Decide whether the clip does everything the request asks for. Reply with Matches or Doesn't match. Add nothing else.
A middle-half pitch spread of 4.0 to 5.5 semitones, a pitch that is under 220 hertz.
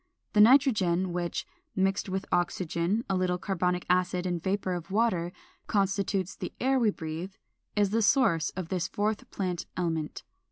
Doesn't match